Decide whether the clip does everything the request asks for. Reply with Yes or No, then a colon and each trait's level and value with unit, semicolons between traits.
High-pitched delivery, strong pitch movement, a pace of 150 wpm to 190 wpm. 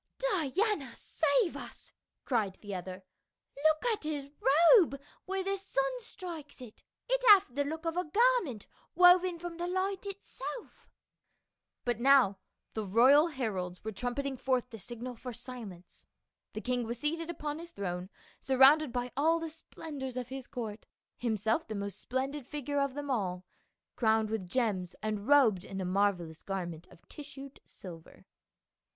Yes: very high, 260 Hz; wide, 6.9 semitones; average, 160 wpm